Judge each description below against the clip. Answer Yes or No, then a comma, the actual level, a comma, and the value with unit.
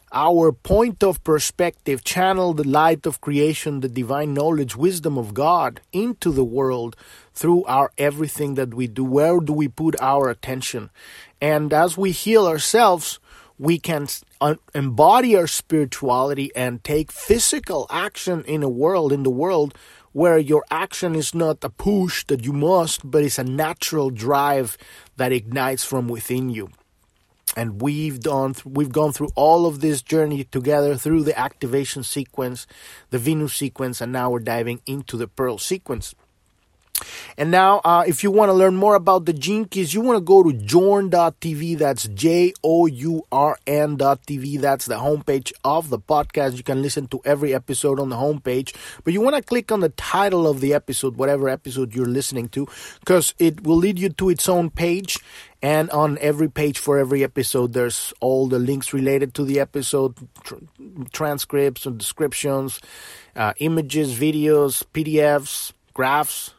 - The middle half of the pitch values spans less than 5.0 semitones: Yes, average, 3.7 semitones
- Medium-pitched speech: Yes, medium, 145 Hz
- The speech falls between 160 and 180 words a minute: Yes, average, 165 wpm